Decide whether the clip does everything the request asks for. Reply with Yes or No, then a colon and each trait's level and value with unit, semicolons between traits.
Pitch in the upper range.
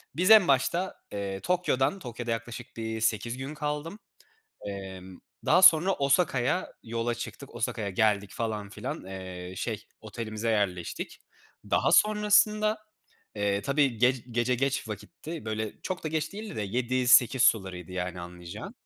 No: low, 120 Hz